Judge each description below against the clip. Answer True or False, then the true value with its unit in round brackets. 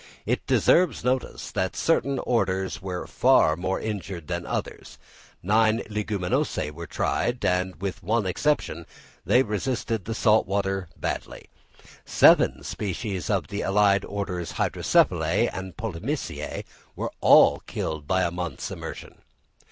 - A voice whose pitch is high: False (95 Hz)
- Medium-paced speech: False (130 wpm)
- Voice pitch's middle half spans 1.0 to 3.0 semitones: False (3.4 semitones)